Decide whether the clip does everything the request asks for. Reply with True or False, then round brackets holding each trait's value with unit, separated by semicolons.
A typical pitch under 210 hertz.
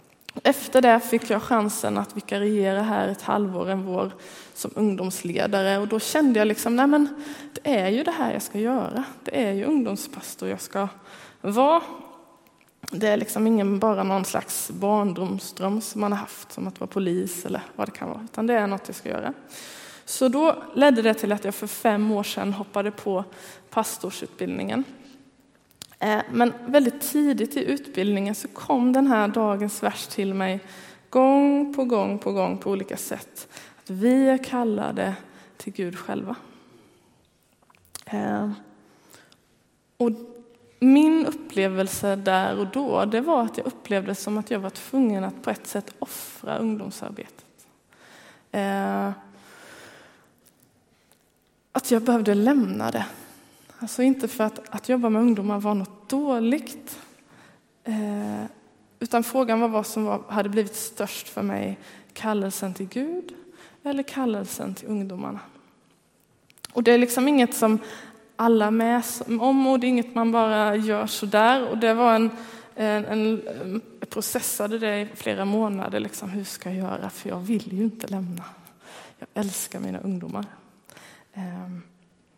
False (220 Hz)